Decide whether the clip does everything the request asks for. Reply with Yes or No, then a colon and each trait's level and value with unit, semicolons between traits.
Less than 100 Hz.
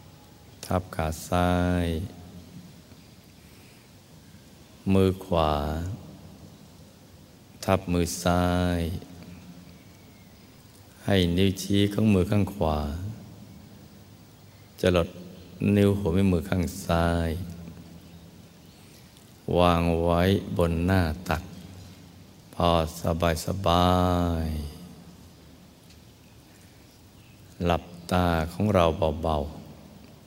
Yes: very low, 90 Hz